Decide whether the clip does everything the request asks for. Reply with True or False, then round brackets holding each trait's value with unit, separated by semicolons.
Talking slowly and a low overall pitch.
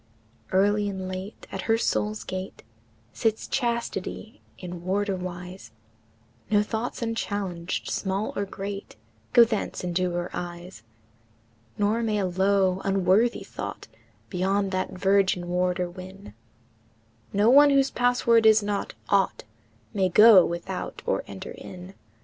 False (125 wpm; 195 Hz)